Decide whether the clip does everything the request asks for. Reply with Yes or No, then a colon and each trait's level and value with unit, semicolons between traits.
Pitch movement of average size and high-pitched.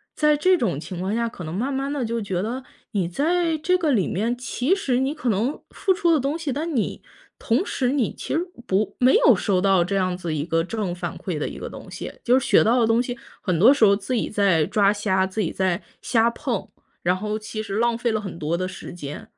No: wide, 5.9 semitones; high, 220 Hz